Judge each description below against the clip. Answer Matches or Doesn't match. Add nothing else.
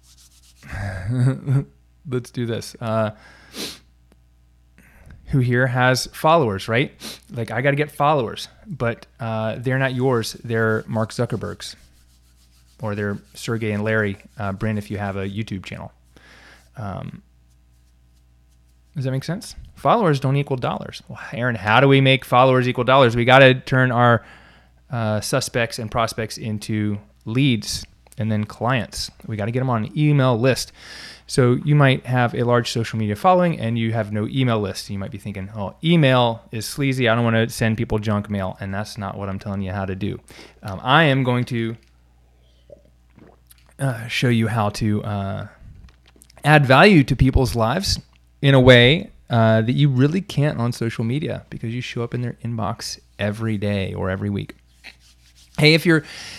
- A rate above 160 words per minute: Matches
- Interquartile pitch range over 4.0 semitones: Matches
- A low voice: Matches